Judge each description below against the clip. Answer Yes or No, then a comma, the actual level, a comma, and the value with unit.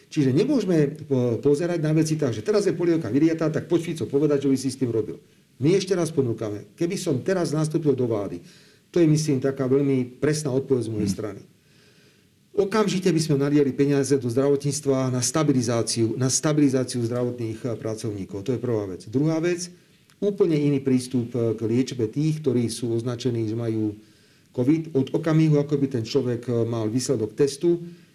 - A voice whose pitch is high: No, low, 135 Hz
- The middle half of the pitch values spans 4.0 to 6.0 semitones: Yes, average, 4.6 semitones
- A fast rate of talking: Yes, fast, 175 wpm